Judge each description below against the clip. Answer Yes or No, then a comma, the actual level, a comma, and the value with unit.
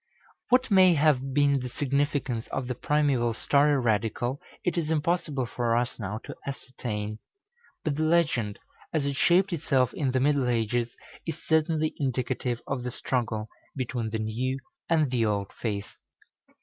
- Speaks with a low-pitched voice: Yes, low, 130 Hz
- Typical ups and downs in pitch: Yes, average, 4.1 semitones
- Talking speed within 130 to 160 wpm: Yes, average, 155 wpm